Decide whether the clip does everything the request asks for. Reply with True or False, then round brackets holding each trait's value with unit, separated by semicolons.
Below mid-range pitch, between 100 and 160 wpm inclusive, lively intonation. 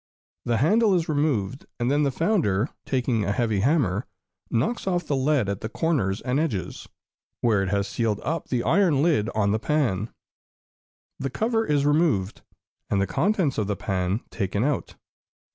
False (125 Hz; 170 wpm; 7.0 semitones)